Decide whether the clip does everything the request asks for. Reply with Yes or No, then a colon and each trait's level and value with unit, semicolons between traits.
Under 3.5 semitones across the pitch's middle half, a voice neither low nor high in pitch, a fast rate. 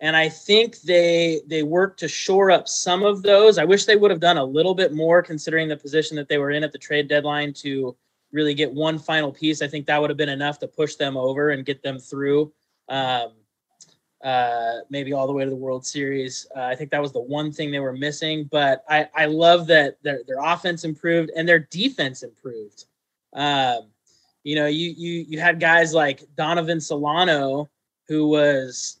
Yes: average, 2.9 semitones; medium, 150 Hz; fast, 210 wpm